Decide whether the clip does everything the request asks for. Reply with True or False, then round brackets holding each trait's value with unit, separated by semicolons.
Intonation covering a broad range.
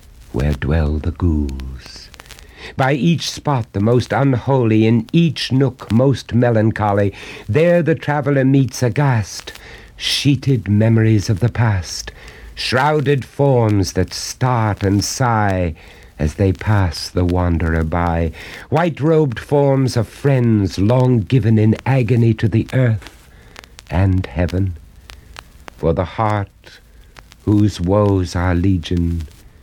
True (6.5 semitones)